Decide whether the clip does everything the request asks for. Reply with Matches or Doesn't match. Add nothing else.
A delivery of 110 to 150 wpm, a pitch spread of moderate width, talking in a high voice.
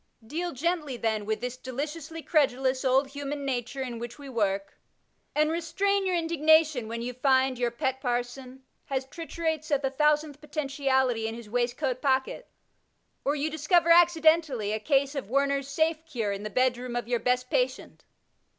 Doesn't match